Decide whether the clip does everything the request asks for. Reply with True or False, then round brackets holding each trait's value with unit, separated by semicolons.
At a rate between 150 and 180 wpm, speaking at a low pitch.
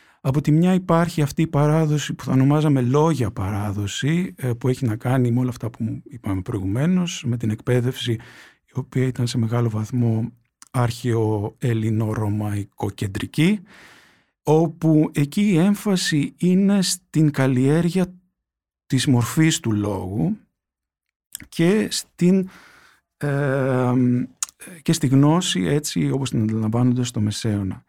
False (120 wpm; 130 Hz)